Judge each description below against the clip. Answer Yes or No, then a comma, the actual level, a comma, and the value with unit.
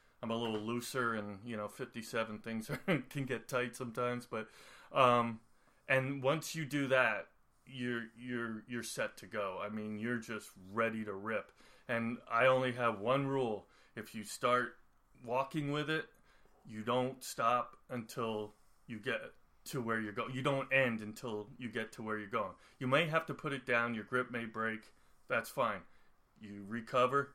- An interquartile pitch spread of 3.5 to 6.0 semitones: No, average, 2.8 semitones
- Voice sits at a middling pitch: No, low, 120 Hz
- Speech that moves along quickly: No, average, 180 wpm